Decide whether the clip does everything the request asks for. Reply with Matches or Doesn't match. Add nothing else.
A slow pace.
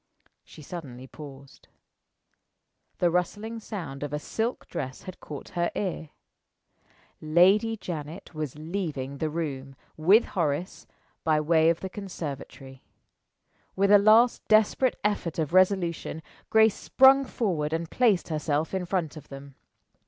Matches